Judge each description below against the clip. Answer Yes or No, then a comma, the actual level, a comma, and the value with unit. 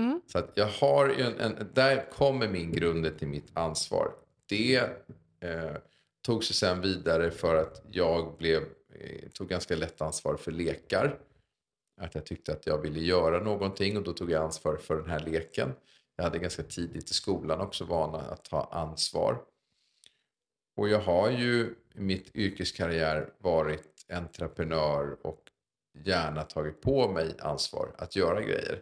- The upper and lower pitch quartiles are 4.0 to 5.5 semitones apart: Yes, average, 4.8 semitones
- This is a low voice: Yes, very low, 85 Hz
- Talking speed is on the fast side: No, average, 160 wpm